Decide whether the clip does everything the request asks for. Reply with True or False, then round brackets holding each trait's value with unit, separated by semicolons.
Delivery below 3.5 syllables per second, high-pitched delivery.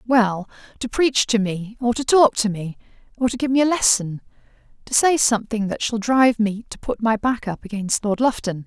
False (5.2 syllables/s; 225 Hz)